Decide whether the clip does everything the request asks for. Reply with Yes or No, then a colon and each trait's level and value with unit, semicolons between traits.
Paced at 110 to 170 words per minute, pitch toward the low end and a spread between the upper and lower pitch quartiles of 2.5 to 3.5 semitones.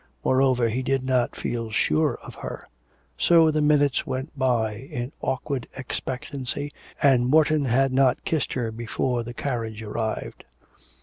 Yes: average, 140 wpm; low, 130 Hz; average, 2.9 semitones